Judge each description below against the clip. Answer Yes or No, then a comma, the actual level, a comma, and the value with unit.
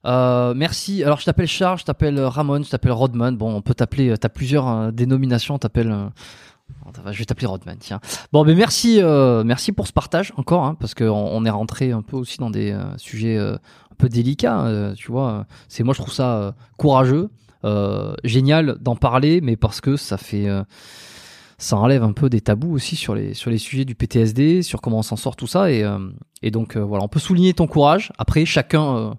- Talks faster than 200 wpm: Yes, fast, 220 wpm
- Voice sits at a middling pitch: No, low, 125 Hz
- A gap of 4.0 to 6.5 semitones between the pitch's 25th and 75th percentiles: Yes, average, 4.7 semitones